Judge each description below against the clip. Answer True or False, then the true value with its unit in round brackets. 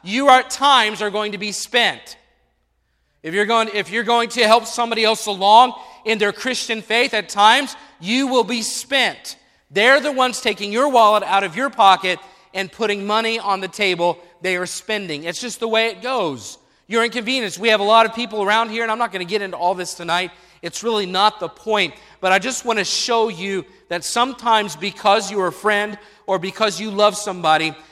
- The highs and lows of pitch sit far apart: False (3.4 semitones)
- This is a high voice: True (210 Hz)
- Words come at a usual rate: False (210 wpm)